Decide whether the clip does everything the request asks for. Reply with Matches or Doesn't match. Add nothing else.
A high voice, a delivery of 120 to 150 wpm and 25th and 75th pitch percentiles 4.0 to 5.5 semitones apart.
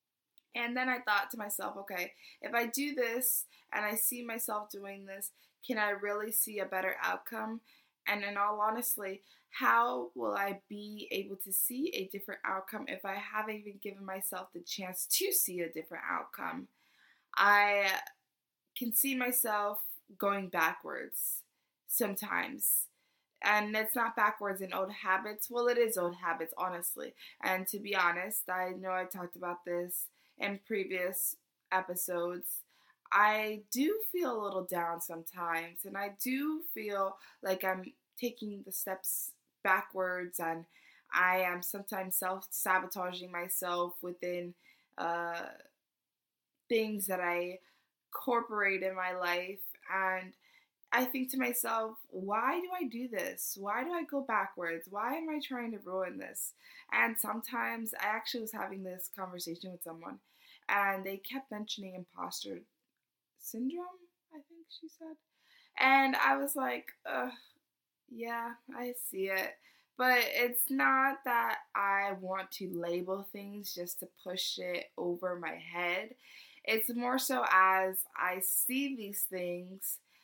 Matches